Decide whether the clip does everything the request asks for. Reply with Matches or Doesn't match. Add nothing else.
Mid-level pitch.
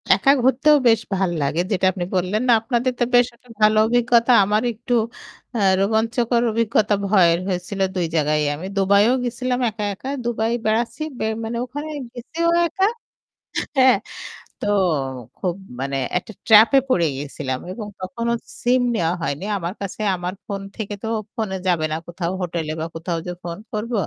Doesn't match